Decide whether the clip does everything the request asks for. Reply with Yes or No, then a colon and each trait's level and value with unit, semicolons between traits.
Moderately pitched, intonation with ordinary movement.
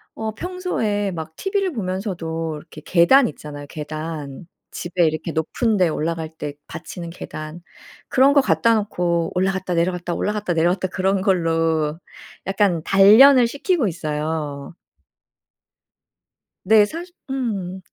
Yes: medium, 180 Hz; average, 4.7 semitones